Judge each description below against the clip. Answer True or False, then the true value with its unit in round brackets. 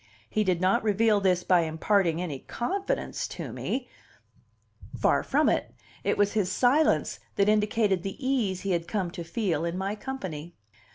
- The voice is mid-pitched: False (195 Hz)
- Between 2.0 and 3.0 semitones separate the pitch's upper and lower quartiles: False (3.6 semitones)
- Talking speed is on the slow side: False (165 wpm)